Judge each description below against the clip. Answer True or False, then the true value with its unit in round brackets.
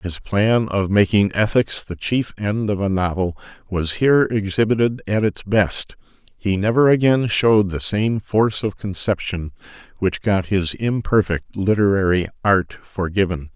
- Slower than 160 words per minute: True (145 wpm)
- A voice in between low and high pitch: False (100 Hz)